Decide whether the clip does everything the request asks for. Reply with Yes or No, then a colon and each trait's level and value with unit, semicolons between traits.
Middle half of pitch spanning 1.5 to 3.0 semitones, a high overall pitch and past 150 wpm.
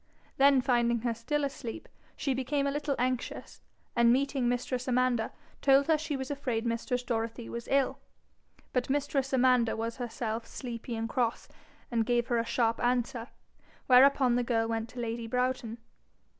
Yes: narrow, 2.4 semitones; high, 245 Hz; average, 160 wpm